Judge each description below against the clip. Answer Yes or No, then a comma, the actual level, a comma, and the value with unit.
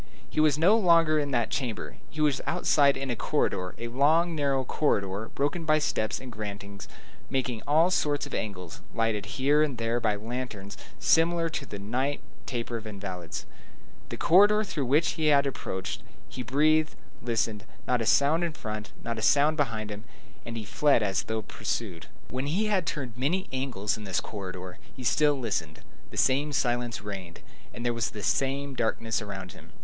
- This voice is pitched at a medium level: No, low, 125 Hz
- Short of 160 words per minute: No, average, 185 wpm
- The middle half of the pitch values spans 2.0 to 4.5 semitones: No, wide, 5.6 semitones